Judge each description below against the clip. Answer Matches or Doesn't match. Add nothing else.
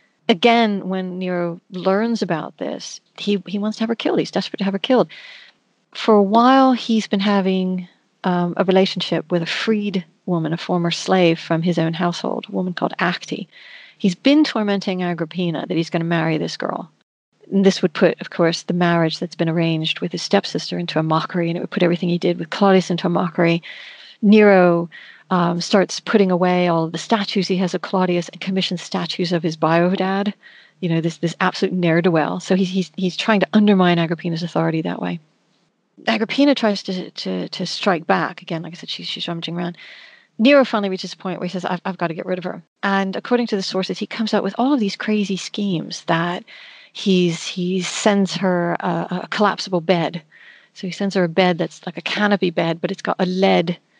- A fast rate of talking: Matches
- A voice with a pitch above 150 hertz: Matches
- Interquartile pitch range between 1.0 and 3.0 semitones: Matches